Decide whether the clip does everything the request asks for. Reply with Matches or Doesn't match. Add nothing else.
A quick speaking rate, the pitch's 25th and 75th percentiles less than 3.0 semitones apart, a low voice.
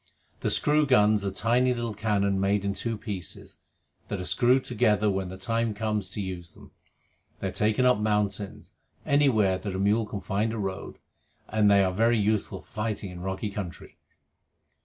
Doesn't match